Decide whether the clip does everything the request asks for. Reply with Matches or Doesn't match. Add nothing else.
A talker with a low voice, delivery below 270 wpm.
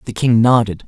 Matches